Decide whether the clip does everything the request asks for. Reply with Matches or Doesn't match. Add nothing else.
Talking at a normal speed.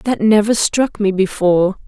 Matches